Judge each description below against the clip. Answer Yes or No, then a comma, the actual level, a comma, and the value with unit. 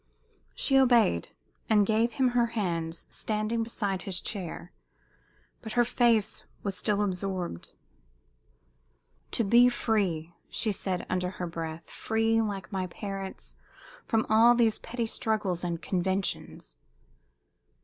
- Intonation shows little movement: No, average, 3.8 semitones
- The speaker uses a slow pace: Yes, slow, 120 wpm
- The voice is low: No, high, 205 Hz